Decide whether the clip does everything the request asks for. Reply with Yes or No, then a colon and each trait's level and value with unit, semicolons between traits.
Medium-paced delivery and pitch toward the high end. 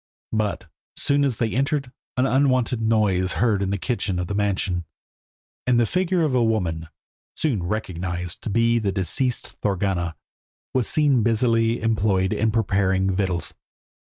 No: average, 155 wpm; low, 110 Hz